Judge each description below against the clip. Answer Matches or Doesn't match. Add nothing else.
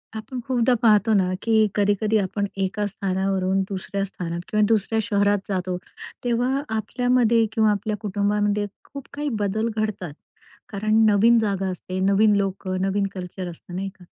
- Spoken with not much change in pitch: Matches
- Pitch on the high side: Matches